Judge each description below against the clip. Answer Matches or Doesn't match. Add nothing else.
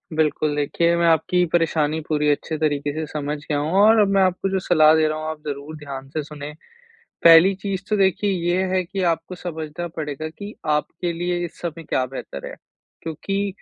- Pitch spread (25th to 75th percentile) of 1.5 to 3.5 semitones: Matches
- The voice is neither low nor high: Matches